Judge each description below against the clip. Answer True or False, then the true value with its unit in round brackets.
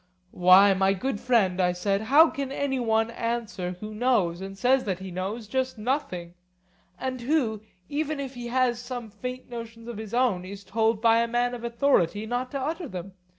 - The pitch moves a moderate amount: True (4.4 semitones)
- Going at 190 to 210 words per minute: True (195 wpm)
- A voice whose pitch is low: False (230 Hz)